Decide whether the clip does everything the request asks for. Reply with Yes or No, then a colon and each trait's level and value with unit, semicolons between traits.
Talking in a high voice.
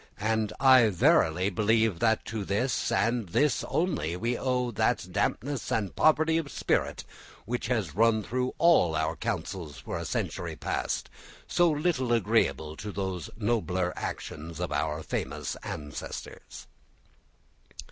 No: low, 110 Hz